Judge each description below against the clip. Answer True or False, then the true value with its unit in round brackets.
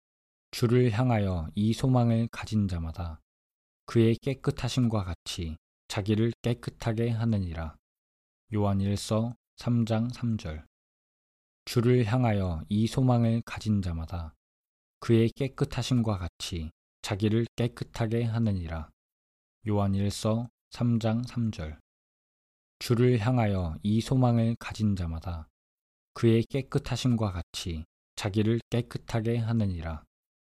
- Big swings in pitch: True (5.9 semitones)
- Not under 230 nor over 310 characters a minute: False (220 characters per minute)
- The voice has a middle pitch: False (110 Hz)